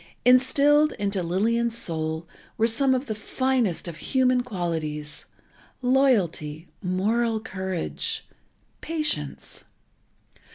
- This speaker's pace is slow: Yes, slow, 90 wpm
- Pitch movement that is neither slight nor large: No, wide, 6.9 semitones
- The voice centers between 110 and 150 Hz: No, high, 220 Hz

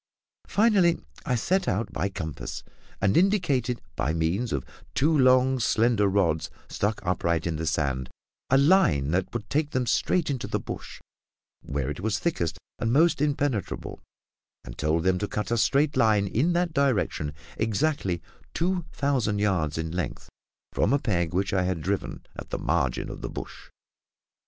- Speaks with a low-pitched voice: Yes, low, 105 Hz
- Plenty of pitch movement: Yes, wide, 8.6 semitones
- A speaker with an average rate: Yes, average, 165 wpm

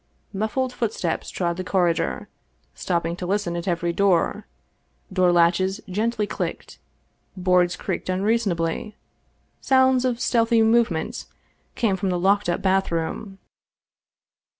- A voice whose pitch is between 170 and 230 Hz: Yes, high, 190 Hz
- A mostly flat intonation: No, average, 4.2 semitones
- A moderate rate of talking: No, slow, 115 wpm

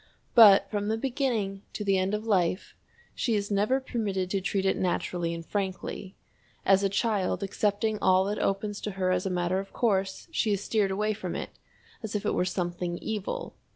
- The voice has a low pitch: No, high, 195 Hz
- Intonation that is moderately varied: No, narrow, 2.2 semitones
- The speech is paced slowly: No, average, 195 wpm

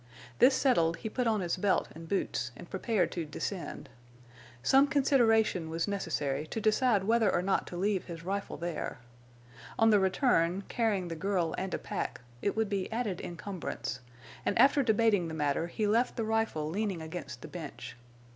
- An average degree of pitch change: Yes, average, 4.8 semitones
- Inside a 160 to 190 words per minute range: Yes, average, 175 wpm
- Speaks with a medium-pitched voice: No, high, 195 Hz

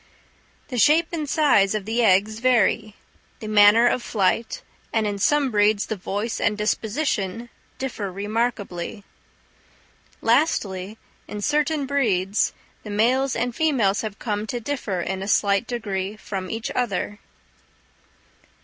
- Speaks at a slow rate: Yes, slow, 130 wpm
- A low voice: No, high, 215 Hz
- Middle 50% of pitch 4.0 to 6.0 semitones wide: No, average, 3.5 semitones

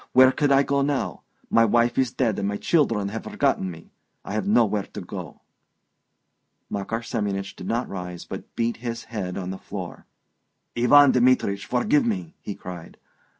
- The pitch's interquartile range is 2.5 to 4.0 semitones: No, average, 4.7 semitones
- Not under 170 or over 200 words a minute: Yes, average, 175 wpm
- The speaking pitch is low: Yes, low, 115 Hz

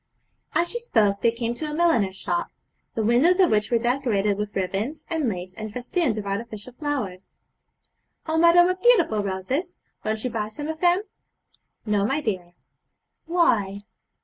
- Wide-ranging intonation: Yes, wide, 7.7 semitones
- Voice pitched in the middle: No, high, 235 Hz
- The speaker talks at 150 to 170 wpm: Yes, average, 165 wpm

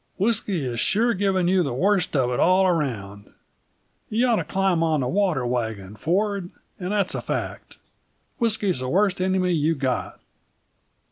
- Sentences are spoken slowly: No, average, 160 wpm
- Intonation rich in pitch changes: Yes, wide, 7.3 semitones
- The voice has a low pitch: No, medium, 180 Hz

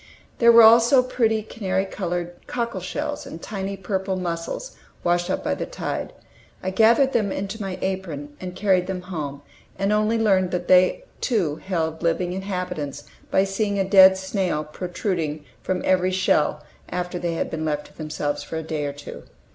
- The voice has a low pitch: No, medium, 185 Hz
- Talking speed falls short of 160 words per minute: No, average, 175 wpm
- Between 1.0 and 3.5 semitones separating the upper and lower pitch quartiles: Yes, average, 3.2 semitones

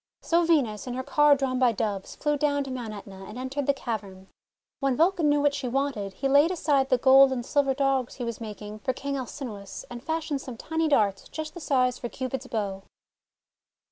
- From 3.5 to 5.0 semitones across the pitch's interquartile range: Yes, average, 3.9 semitones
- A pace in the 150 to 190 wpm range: No, fast, 205 wpm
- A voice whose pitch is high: Yes, very high, 260 Hz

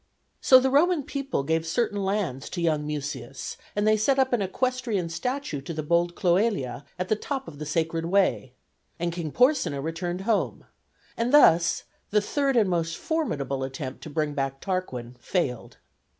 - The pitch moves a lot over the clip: Yes, wide, 7.4 semitones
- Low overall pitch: No, medium, 175 Hz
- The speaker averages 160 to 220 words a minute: Yes, average, 170 wpm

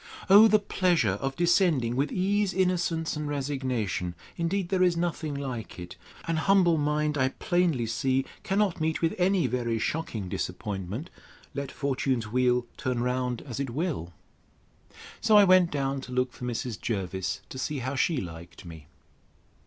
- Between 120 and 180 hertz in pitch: Yes, medium, 140 Hz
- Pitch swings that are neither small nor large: No, wide, 6.2 semitones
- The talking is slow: No, average, 155 wpm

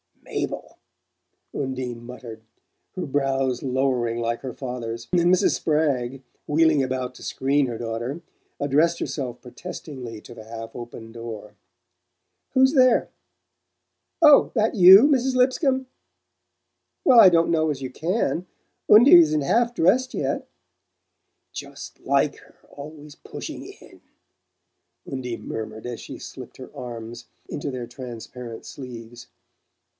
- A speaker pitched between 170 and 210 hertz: No, low, 135 Hz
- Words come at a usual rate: No, slow, 125 wpm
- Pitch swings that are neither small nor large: No, wide, 6.1 semitones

